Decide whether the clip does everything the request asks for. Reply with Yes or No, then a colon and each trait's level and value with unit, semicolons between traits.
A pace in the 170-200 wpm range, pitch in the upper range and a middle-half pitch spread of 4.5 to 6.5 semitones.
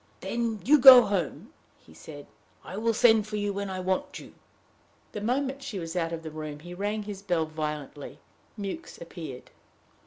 Yes: average, 180 wpm; high, 195 Hz; average, 5.3 semitones